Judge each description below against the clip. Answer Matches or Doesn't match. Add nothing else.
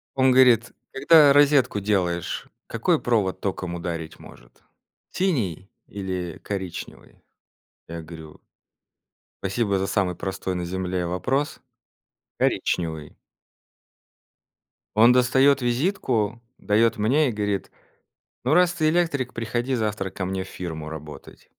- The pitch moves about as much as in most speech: Doesn't match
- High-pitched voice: Doesn't match